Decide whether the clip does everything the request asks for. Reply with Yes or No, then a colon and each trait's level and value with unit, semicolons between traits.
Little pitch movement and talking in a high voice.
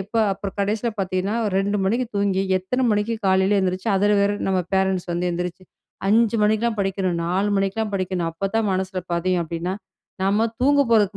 Yes: narrow, 2.0 semitones; high, 195 Hz